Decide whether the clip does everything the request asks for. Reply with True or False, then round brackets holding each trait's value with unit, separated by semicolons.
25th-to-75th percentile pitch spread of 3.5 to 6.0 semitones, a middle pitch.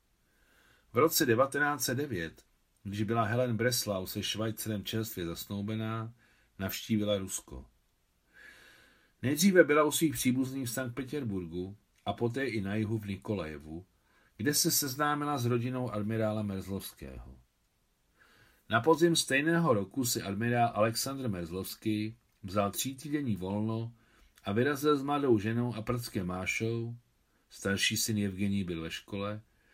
False (4.1 semitones; 110 Hz)